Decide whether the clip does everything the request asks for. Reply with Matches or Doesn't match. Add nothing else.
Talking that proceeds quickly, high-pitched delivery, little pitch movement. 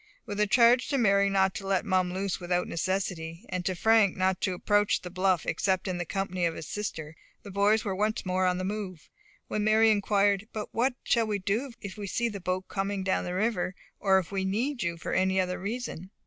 Matches